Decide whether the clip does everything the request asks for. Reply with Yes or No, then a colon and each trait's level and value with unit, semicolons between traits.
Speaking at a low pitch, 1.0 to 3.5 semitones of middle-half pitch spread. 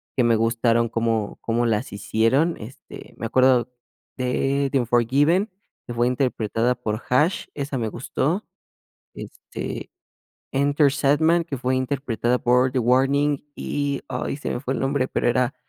Yes: low, 130 Hz; average, 3.1 semitones